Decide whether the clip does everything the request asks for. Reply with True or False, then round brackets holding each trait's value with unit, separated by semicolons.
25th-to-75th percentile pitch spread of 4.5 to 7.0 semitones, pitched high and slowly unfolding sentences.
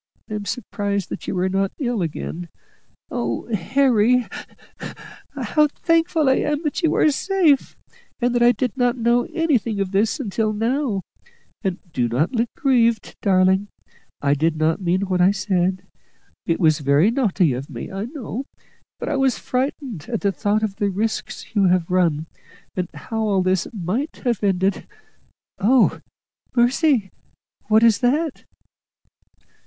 False (5.2 semitones; 210 Hz; 160 wpm)